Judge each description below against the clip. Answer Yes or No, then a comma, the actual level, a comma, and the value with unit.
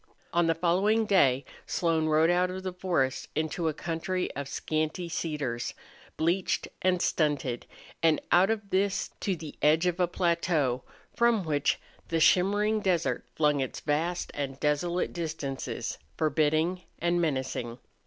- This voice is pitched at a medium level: Yes, medium, 165 Hz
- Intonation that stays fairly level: No, average, 3.5 semitones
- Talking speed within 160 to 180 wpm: No, average, 145 wpm